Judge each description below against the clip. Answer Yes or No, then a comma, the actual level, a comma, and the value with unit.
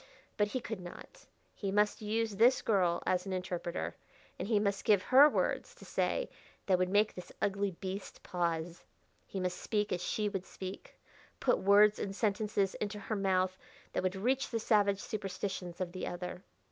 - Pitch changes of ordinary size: No, narrow, 2.3 semitones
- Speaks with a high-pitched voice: Yes, high, 195 Hz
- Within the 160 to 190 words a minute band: Yes, average, 180 wpm